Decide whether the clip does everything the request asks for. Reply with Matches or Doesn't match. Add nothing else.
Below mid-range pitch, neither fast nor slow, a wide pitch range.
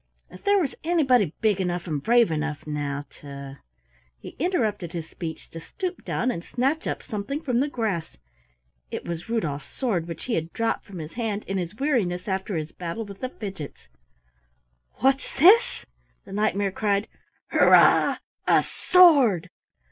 Doesn't match